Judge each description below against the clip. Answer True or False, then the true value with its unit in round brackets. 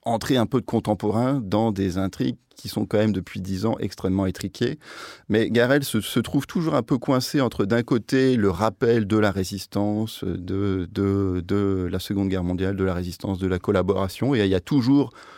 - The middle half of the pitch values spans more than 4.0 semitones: False (3.7 semitones)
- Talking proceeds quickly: False (205 wpm)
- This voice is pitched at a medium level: False (105 Hz)